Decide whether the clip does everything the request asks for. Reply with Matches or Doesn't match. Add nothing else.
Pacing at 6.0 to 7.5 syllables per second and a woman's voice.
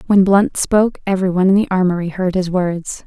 Matches